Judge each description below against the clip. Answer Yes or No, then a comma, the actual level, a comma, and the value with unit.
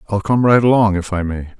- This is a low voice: Yes, low, 100 Hz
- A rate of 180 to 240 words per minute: No, fast, 265 wpm